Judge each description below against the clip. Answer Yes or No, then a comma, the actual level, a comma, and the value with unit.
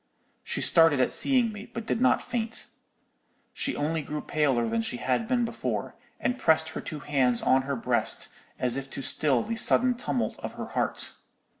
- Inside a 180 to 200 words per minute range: Yes, average, 185 wpm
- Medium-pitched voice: Yes, medium, 150 Hz